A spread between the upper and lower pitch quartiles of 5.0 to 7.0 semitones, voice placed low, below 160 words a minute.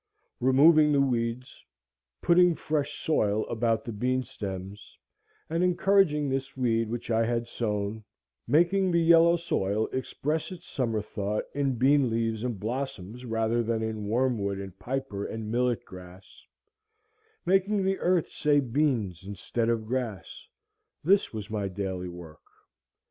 Yes: wide, 5.5 semitones; low, 120 Hz; slow, 135 wpm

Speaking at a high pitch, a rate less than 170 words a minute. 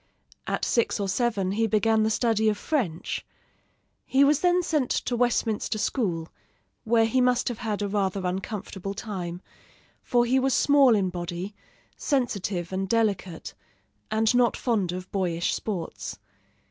Yes: high, 215 Hz; average, 145 wpm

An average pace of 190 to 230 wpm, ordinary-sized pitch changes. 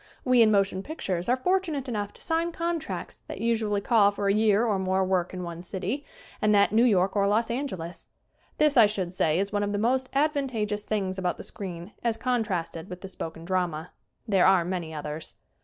Yes: fast, 205 wpm; average, 4.3 semitones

